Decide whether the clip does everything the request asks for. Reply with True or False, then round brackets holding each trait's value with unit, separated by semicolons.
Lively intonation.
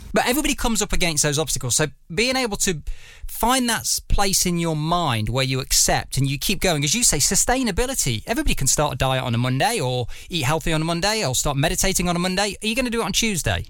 True (7.3 semitones)